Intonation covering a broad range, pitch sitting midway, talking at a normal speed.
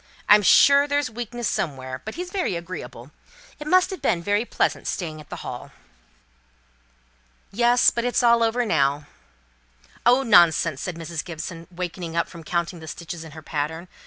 Yes: wide, 6.7 semitones; medium, 175 Hz; average, 165 wpm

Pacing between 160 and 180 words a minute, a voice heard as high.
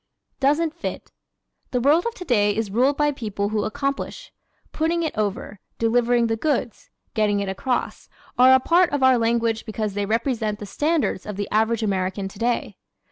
Yes: average, 175 wpm; high, 230 Hz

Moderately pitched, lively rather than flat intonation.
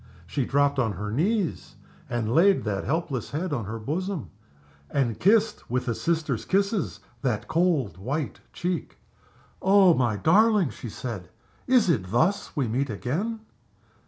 Yes: medium, 145 Hz; wide, 8.0 semitones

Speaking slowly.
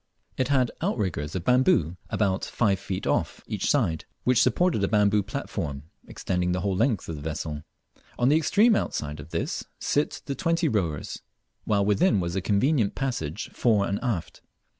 No: average, 170 wpm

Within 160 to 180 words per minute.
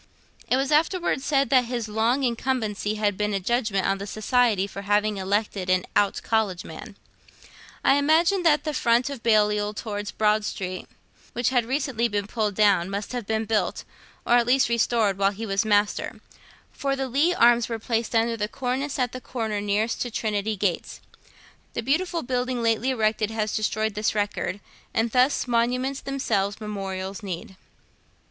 Yes: average, 170 wpm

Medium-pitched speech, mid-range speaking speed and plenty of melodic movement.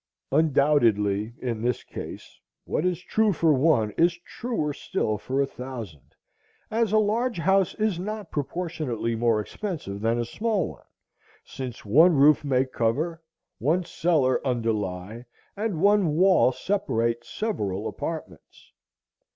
No: medium, 145 Hz; slow, 130 wpm; wide, 7.7 semitones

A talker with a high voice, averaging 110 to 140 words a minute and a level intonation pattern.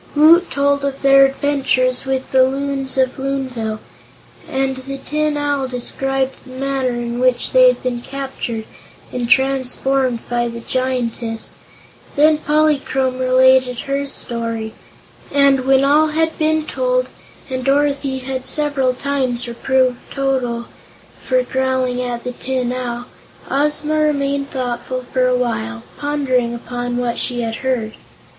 Yes: very high, 260 Hz; slow, 135 wpm; narrow, 2.1 semitones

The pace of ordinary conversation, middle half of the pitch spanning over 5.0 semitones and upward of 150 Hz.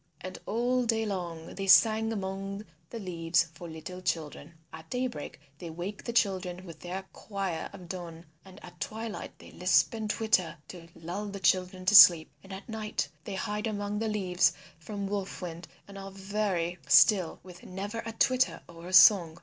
No: average, 180 wpm; average, 3.3 semitones; high, 190 Hz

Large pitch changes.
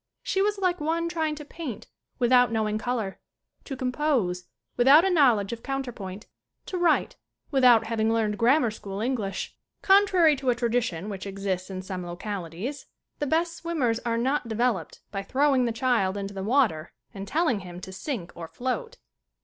Yes: wide, 6.7 semitones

